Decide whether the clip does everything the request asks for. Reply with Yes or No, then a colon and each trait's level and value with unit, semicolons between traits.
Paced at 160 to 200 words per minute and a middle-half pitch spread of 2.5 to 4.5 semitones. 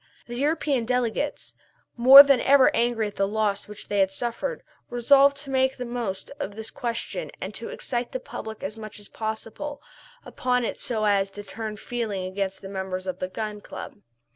Yes: average, 190 wpm; average, 3.9 semitones